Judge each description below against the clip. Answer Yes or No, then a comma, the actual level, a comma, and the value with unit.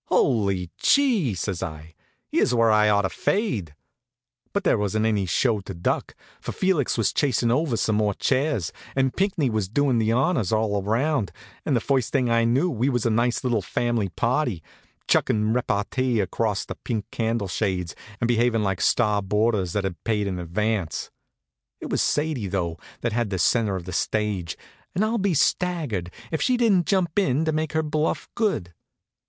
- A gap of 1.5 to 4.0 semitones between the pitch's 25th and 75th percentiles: No, wide, 5.6 semitones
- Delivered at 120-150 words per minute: No, average, 180 wpm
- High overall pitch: No, low, 115 Hz